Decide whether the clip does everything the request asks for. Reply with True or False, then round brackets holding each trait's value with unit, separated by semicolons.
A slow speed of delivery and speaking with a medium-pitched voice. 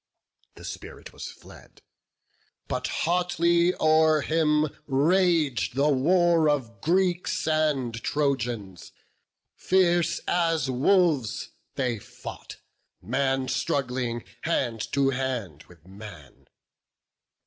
True (95 wpm; 145 Hz)